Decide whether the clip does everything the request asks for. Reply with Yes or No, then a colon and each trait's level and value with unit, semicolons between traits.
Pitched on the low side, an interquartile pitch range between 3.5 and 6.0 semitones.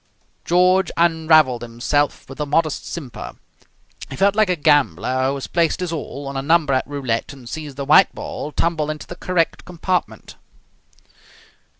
No: medium, 150 Hz; average, 3.8 semitones